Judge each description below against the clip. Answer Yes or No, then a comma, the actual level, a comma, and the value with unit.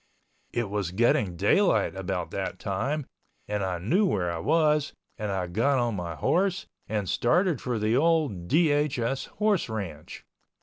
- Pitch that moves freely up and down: Yes, wide, 8.0 semitones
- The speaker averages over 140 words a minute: Yes, average, 150 wpm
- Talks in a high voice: No, low, 115 Hz